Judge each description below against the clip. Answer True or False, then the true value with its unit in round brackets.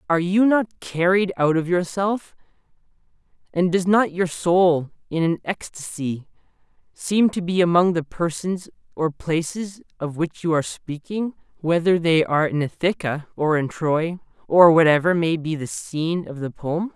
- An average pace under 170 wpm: True (160 wpm)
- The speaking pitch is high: False (170 Hz)